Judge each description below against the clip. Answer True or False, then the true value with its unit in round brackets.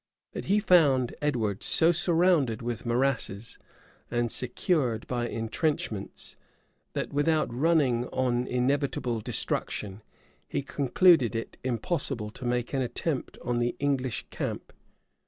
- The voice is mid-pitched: False (125 Hz)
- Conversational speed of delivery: False (120 wpm)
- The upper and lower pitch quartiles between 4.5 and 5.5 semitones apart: False (3.9 semitones)